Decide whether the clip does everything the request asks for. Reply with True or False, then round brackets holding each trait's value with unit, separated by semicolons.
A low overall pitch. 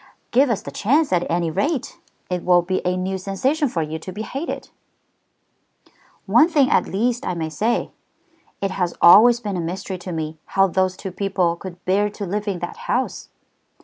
False (190 Hz)